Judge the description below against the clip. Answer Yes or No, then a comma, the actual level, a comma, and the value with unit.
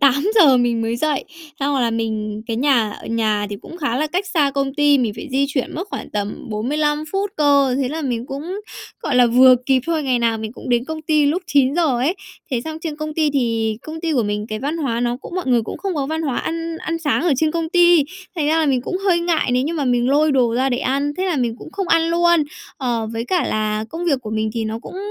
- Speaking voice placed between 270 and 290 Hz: Yes, very high, 280 Hz